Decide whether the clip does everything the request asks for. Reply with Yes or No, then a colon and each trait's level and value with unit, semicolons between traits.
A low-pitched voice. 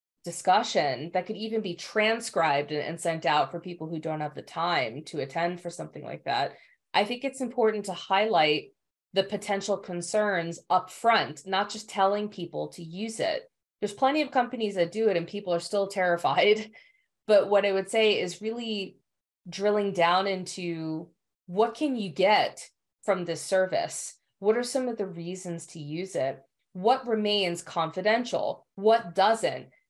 No: high, 195 Hz